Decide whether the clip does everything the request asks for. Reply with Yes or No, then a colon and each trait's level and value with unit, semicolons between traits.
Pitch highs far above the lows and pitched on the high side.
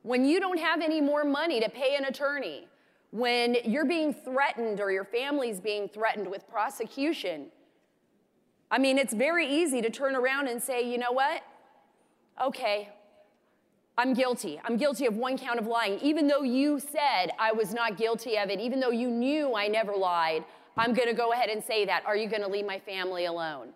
No: average, 4.4 semitones; high, 245 Hz